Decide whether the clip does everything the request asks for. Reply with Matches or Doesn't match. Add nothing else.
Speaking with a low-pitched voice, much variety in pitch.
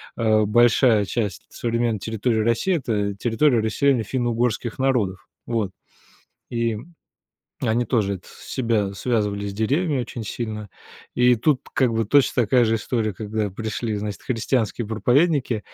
Doesn't match